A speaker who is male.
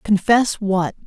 No: female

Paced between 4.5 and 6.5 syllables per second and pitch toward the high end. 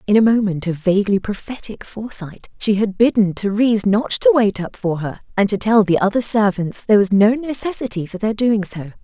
Yes: 5.5 syllables/s; high, 210 Hz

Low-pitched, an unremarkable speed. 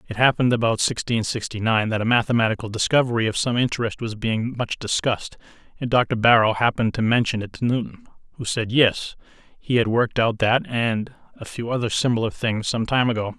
Yes: low, 115 Hz; average, 195 wpm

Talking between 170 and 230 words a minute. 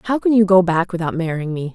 No: fast, 275 wpm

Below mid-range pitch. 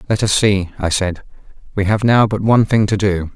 Yes: low, 100 Hz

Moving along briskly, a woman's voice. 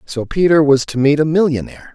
No: fast, 215 wpm; male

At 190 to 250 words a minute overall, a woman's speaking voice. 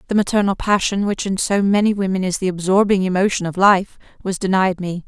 Yes: average, 200 wpm; female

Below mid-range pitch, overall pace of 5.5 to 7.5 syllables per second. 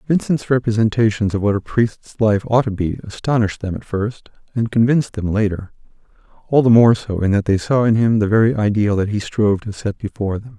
Yes: low, 110 Hz; 5.8 syllables/s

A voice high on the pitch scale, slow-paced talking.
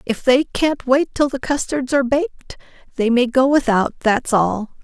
No: very high, 260 Hz; average, 175 wpm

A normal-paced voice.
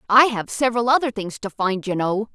No: fast, 230 wpm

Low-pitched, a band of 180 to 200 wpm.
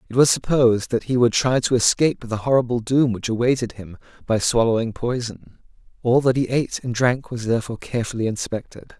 Yes: low, 120 Hz; average, 185 wpm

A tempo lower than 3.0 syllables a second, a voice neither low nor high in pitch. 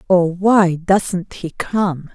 Yes: 2.6 syllables/s; medium, 180 Hz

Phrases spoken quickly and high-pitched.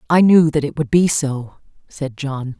No: fast, 210 wpm; medium, 145 Hz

